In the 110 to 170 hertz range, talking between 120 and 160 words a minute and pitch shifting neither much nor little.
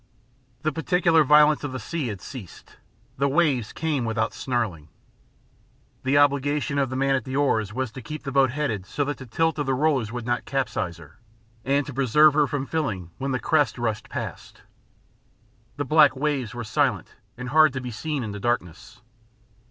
No: low, 135 Hz; average, 190 wpm; average, 3.6 semitones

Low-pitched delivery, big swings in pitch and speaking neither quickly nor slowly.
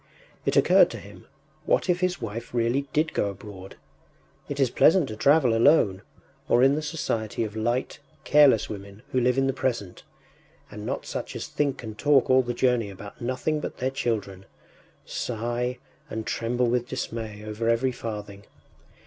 No: low, 120 Hz; average, 3.7 semitones; average, 170 wpm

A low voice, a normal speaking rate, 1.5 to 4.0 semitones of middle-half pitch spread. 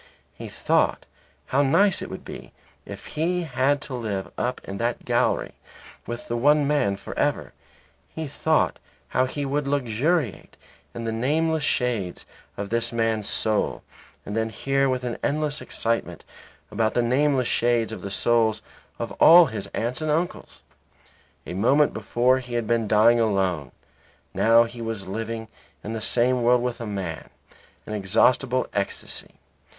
Yes: low, 120 Hz; average, 155 wpm; average, 3.7 semitones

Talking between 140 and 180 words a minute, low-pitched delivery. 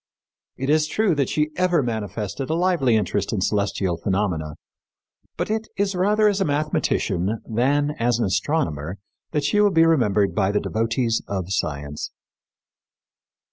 Yes: average, 150 wpm; low, 120 Hz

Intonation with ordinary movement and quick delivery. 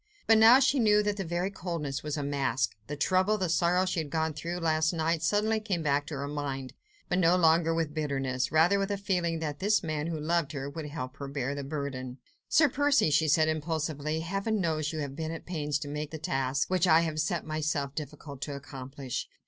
Yes: average, 3.6 semitones; fast, 230 wpm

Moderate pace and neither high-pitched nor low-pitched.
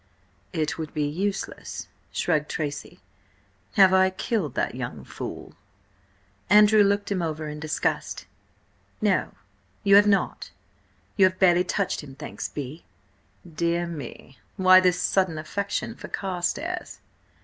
No: slow, 125 wpm; medium, 175 Hz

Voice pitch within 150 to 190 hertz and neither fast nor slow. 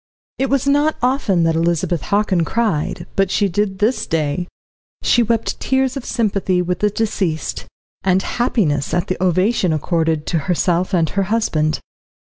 Yes: medium, 185 Hz; average, 155 wpm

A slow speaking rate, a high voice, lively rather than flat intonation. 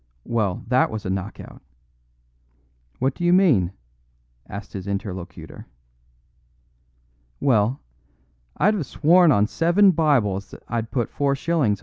No: slow, 120 wpm; low, 120 Hz; wide, 8.1 semitones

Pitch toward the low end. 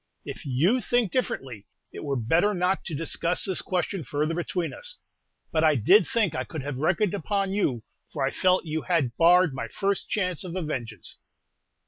No: medium, 170 Hz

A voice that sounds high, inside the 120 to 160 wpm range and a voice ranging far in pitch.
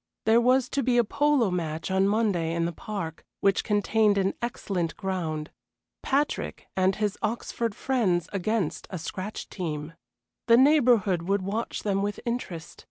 No: high, 200 Hz; average, 155 wpm; average, 4.6 semitones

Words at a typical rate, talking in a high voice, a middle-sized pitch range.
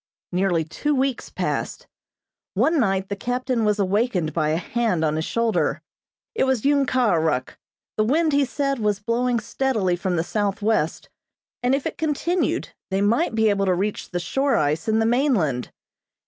No: average, 175 wpm; high, 215 Hz; wide, 6.0 semitones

